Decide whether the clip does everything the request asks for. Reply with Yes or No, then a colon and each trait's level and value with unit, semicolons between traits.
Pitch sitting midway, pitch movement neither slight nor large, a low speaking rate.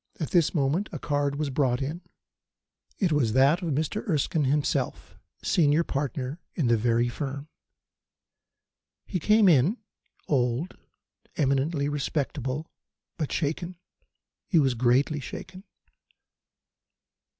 Yes: medium, 145 Hz; average, 3.5 semitones; slow, 115 wpm